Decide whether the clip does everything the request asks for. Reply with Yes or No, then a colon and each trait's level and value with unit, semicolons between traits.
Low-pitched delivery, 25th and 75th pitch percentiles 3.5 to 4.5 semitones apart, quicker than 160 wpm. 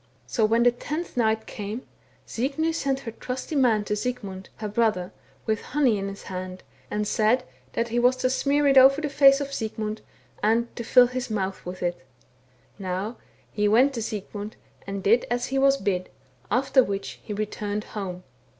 No: high, 225 Hz; average, 3.9 semitones; average, 180 wpm